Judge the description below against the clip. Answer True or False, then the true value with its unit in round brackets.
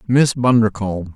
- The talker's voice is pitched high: False (115 Hz)